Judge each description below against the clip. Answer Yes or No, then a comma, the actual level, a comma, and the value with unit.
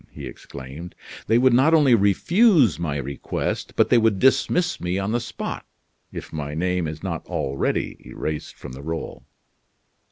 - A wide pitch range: Yes, wide, 8.0 semitones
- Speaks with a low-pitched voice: Yes, very low, 95 Hz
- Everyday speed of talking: Yes, average, 160 wpm